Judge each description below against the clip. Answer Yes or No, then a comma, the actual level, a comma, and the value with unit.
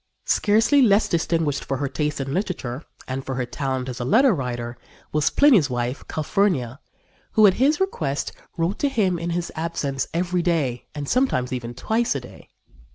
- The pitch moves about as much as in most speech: No, wide, 7.1 semitones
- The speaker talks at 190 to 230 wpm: No, average, 180 wpm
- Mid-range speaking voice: Yes, medium, 155 Hz